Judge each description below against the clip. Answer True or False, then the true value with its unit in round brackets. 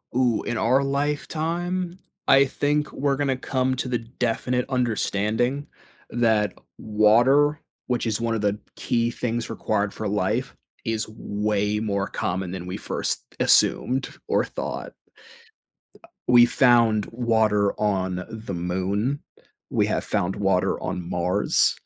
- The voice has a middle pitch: False (115 Hz)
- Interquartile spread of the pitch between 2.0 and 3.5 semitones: False (4.0 semitones)